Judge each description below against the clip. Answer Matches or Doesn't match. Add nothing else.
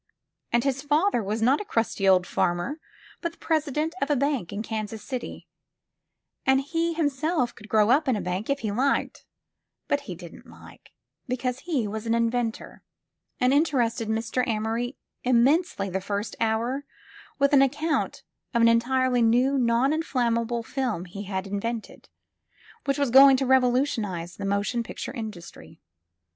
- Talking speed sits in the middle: Matches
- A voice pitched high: Matches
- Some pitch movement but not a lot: Matches